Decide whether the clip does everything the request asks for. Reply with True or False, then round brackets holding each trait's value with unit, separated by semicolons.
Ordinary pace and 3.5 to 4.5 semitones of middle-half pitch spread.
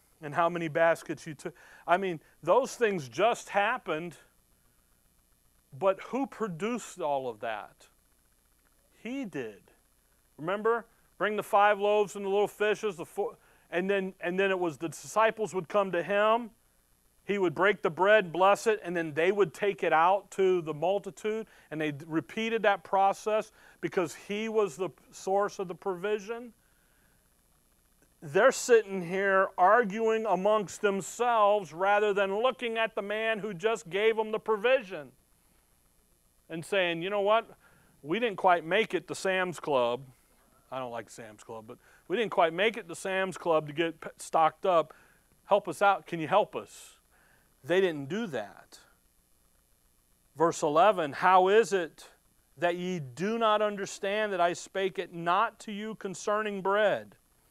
True (160 wpm; 4.0 semitones)